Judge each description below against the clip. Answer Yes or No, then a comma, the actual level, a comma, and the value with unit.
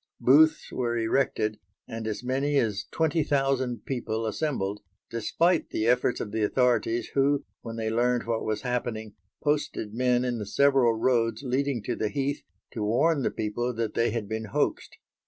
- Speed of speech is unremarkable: Yes, average, 170 wpm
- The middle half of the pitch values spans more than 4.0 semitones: No, average, 3.6 semitones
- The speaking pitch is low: Yes, low, 120 Hz